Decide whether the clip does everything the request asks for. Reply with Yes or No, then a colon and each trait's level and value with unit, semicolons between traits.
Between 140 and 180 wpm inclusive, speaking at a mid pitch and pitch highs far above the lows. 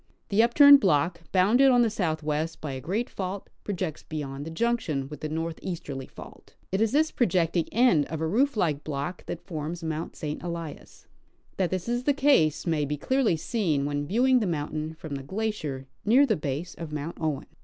No: average, 190 wpm; medium, 165 Hz; wide, 6.4 semitones